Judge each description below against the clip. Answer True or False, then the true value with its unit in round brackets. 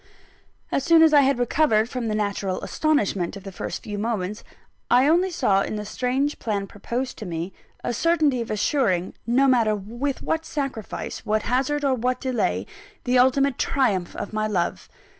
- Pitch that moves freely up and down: False (4.7 semitones)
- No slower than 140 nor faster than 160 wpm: False (180 wpm)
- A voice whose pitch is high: True (240 Hz)